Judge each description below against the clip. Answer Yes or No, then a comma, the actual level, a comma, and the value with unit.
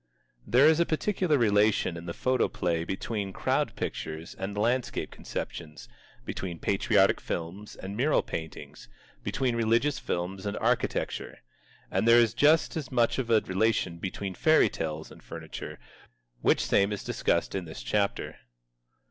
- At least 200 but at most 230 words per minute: No, average, 145 wpm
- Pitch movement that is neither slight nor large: No, wide, 6.0 semitones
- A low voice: Yes, low, 105 Hz